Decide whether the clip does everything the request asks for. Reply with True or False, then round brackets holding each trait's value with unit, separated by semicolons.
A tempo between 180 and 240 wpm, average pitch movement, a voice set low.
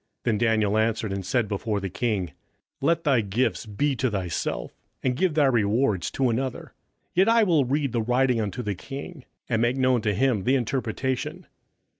True (185 wpm; 4.1 semitones; 120 Hz)